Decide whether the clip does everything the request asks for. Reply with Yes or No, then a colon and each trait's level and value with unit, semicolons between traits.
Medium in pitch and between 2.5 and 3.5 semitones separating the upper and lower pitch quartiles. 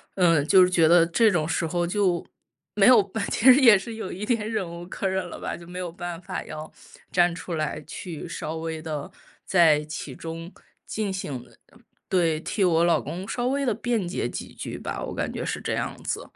Yes: medium, 175 Hz; average, 3.2 semitones